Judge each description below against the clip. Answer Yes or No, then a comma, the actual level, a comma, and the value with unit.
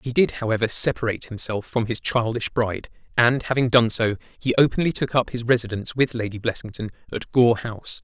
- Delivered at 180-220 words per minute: Yes, average, 185 wpm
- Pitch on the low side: Yes, low, 115 Hz